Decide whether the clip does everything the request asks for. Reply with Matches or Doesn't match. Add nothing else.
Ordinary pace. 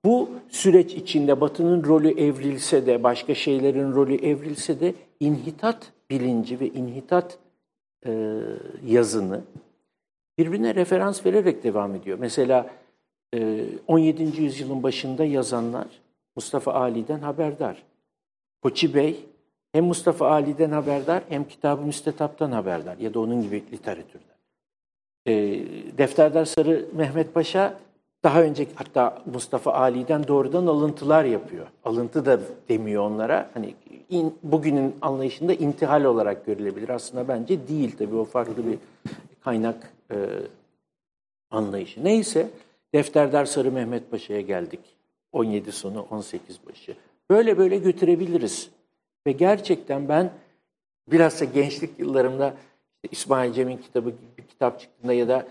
Doesn't match